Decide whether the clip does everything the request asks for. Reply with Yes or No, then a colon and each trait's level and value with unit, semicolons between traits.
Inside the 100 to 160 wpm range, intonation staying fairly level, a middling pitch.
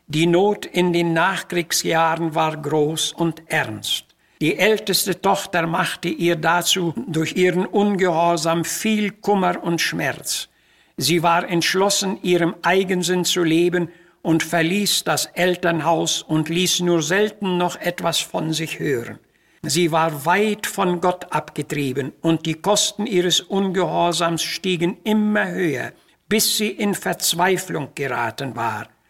Yes: average, 130 wpm; narrow, 2.3 semitones; medium, 175 Hz